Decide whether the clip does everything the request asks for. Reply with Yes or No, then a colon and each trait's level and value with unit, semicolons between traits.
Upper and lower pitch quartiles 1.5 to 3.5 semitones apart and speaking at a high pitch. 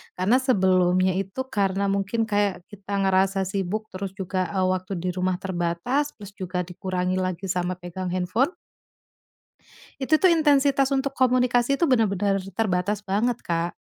No: average, 4.1 semitones; high, 195 Hz